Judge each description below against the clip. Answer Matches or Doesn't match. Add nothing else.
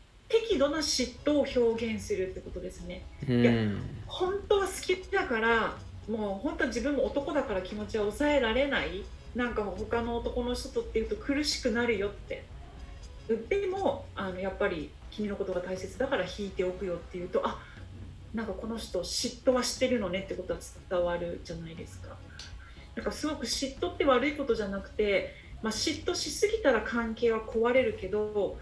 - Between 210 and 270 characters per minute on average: Doesn't match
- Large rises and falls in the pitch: Matches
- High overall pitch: Matches